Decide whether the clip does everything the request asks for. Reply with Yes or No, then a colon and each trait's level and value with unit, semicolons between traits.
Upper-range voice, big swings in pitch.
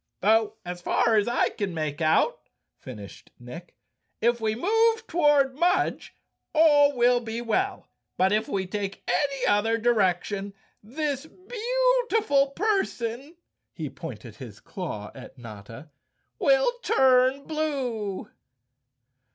Yes: high, 240 Hz; wide, 7.7 semitones